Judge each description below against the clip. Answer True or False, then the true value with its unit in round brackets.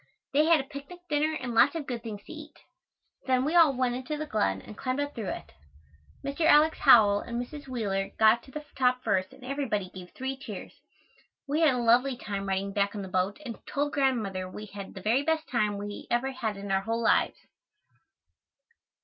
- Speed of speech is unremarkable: False (210 wpm)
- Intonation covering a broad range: True (5.7 semitones)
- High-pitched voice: True (245 Hz)